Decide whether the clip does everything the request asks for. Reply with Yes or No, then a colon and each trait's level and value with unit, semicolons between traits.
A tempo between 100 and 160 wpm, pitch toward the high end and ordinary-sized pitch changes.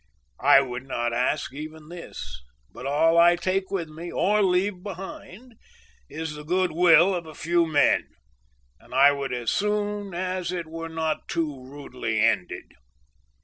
No: average, 155 wpm; medium, 165 Hz; average, 4.4 semitones